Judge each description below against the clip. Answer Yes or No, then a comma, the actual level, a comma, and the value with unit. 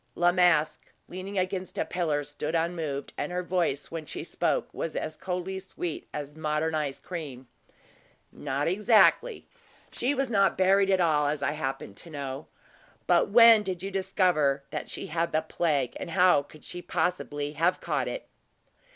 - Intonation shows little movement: No, average, 3.9 semitones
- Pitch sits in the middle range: Yes, medium, 170 Hz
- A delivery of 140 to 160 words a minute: No, average, 170 wpm